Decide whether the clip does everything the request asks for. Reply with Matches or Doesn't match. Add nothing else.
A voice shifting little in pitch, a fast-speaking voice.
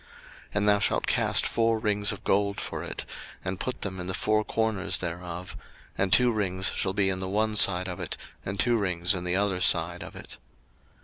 Matches